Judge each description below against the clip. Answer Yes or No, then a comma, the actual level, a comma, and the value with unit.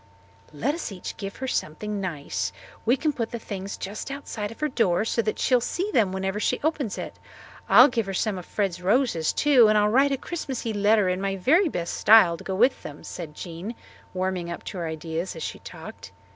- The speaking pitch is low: No, high, 210 Hz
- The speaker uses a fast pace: Yes, fast, 220 wpm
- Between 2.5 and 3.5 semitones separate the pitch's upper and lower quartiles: No, average, 5.3 semitones